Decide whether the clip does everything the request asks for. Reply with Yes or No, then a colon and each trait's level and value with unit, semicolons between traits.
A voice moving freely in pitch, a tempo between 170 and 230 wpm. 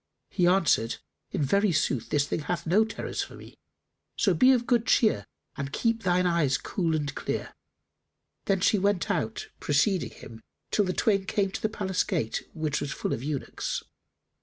Yes: wide, 5.8 semitones; average, 180 wpm